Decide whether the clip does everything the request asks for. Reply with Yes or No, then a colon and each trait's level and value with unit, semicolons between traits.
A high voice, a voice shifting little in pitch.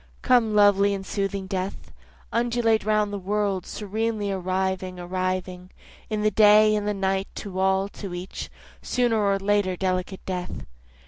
Yes: high, 200 Hz; narrow, 2.1 semitones